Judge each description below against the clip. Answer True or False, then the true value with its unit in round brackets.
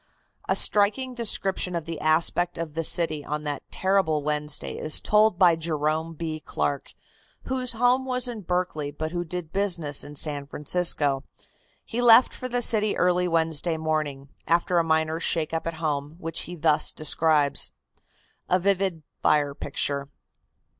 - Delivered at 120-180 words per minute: True (155 wpm)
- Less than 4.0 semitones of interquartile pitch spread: True (3.6 semitones)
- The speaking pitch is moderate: True (165 Hz)